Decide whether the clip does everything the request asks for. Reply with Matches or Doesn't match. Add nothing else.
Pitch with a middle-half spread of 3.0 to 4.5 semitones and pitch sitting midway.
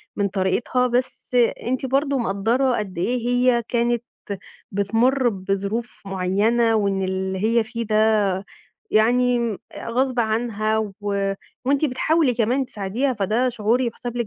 Doesn't match